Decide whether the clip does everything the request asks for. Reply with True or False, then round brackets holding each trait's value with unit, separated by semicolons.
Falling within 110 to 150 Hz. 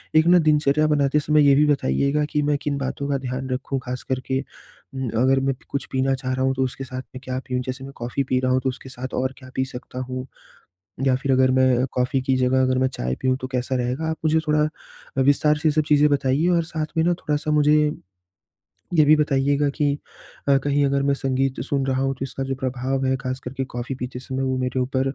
True (135 Hz)